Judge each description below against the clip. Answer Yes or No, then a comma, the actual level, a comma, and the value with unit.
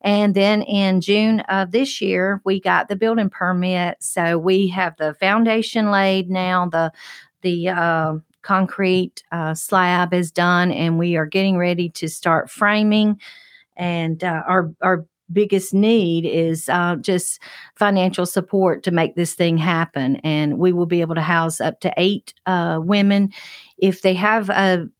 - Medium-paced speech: Yes, average, 160 wpm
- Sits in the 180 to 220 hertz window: Yes, medium, 185 Hz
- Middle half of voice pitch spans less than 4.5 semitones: Yes, average, 2.8 semitones